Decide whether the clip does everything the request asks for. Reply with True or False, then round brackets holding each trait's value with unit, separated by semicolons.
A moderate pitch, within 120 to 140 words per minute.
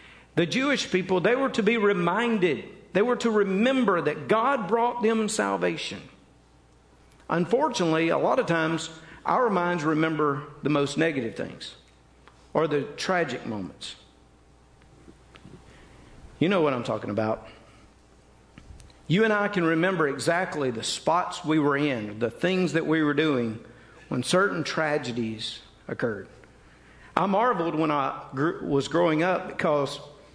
True (160 Hz; 135 wpm)